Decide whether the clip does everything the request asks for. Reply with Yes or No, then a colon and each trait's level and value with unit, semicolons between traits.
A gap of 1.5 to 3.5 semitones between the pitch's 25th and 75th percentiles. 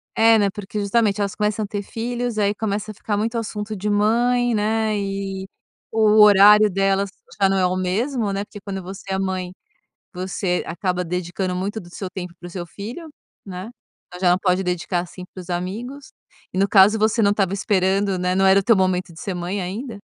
Yes: narrow, 2.5 semitones